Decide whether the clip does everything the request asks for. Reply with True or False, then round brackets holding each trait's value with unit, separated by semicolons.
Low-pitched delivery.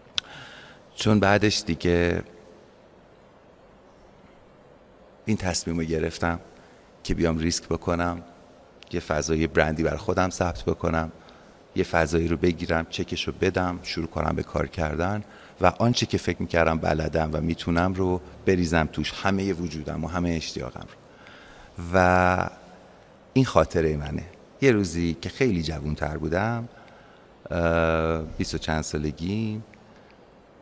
True (85 Hz)